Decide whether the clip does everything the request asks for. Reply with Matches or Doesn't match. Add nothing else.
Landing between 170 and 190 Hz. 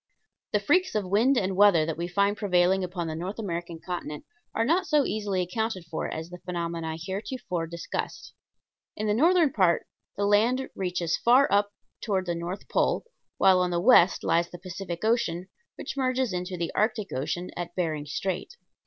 Matches